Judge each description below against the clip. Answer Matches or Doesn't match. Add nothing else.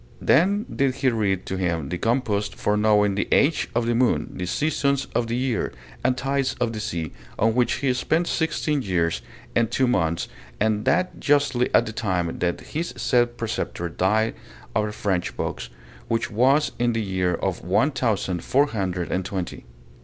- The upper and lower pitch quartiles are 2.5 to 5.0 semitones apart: Doesn't match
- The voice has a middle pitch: Doesn't match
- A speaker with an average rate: Matches